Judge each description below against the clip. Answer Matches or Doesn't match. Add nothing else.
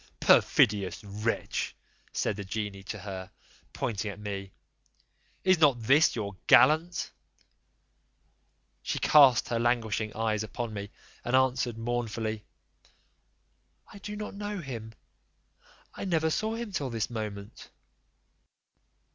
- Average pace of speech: Doesn't match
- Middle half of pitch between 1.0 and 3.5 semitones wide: Doesn't match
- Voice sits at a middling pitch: Doesn't match